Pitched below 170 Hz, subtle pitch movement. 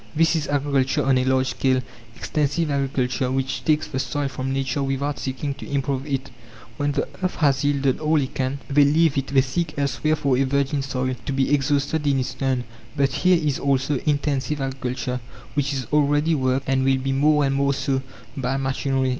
Yes: low, 135 Hz; narrow, 1.6 semitones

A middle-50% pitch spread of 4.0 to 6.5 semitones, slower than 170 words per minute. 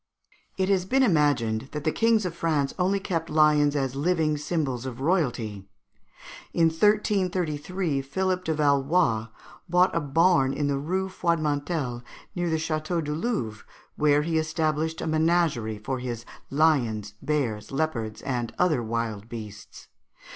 Yes: average, 4.7 semitones; average, 140 wpm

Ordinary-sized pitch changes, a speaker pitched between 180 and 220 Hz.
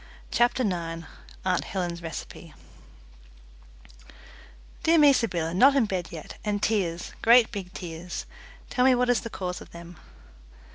No: wide, 5.8 semitones; high, 190 Hz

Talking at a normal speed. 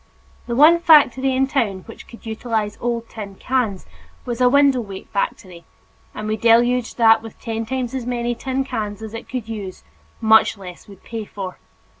Yes: average, 180 wpm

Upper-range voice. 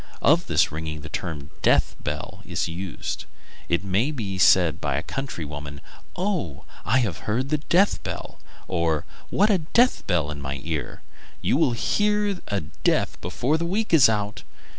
No: low, 100 Hz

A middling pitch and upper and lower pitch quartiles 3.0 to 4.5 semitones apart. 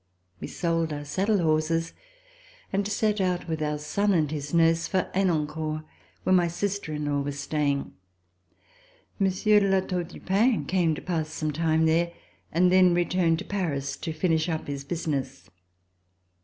Yes: medium, 165 Hz; average, 3.4 semitones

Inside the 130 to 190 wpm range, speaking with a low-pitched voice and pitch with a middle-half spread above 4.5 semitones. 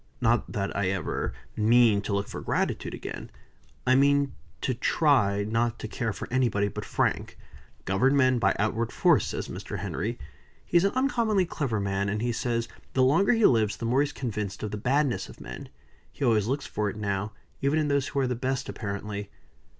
No: average, 200 wpm; low, 120 Hz; average, 5.0 semitones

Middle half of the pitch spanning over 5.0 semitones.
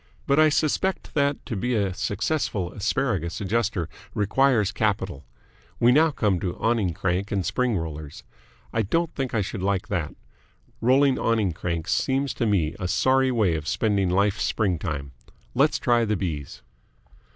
Yes: wide, 5.4 semitones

